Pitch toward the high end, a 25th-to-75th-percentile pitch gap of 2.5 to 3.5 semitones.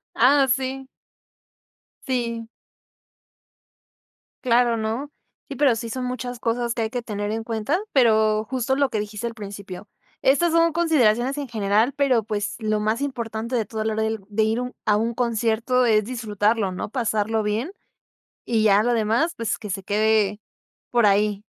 Yes: high, 230 Hz; average, 2.8 semitones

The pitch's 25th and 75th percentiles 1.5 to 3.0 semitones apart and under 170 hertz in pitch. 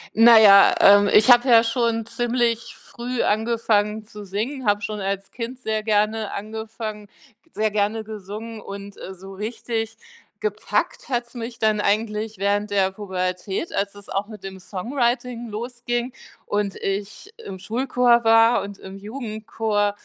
No: narrow, 2.4 semitones; high, 215 Hz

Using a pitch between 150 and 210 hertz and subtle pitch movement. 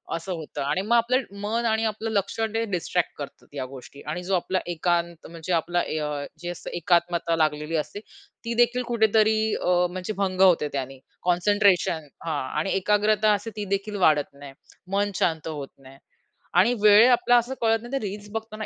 No: medium, 185 Hz; average, 4.9 semitones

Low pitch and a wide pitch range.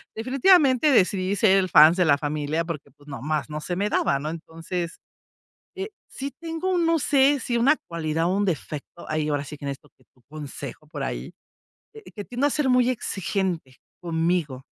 No: medium, 175 Hz; wide, 8.6 semitones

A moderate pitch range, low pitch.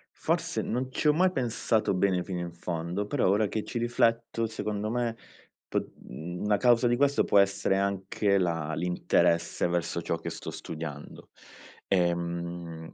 Yes: average, 5.0 semitones; low, 100 Hz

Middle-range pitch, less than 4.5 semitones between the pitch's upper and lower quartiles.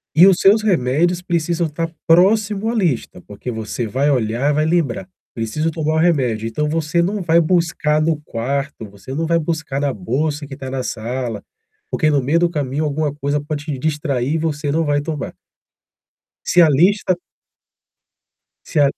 Yes: medium, 150 Hz; average, 3.7 semitones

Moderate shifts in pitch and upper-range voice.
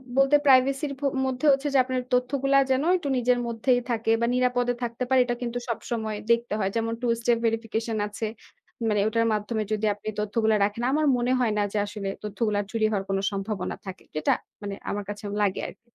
Yes: average, 3.0 semitones; high, 230 Hz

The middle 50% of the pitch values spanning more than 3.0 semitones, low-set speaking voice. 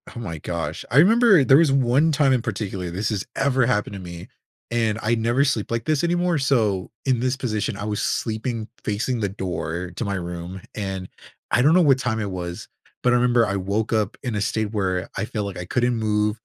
Yes: average, 4.5 semitones; low, 110 Hz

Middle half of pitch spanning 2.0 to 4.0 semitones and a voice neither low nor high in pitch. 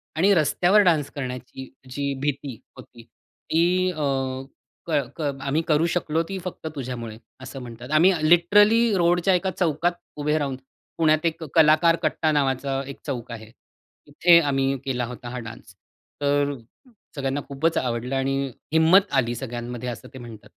No: average, 4.7 semitones; medium, 145 Hz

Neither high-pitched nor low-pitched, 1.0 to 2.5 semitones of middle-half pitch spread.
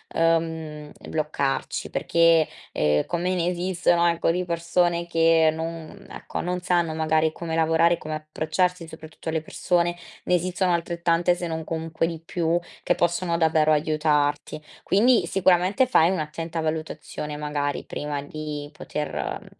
Yes: medium, 165 Hz; narrow, 1.8 semitones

